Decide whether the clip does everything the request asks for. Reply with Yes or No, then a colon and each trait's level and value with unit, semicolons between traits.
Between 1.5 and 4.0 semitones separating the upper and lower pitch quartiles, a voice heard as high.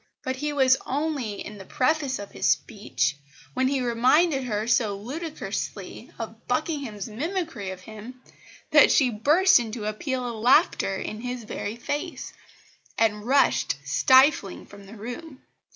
No: average, 4.9 semitones; very high, 250 Hz